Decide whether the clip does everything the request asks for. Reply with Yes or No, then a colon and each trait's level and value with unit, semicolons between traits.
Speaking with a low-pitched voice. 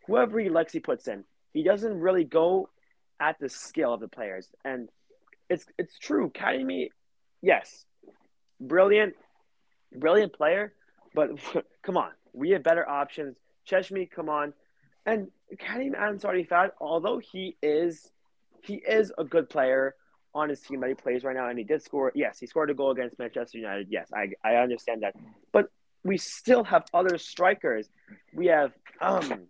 No: medium, 165 Hz